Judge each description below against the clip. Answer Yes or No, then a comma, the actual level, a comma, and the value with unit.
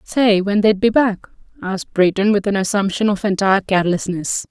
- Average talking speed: Yes, average, 175 wpm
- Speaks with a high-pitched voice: Yes, high, 200 Hz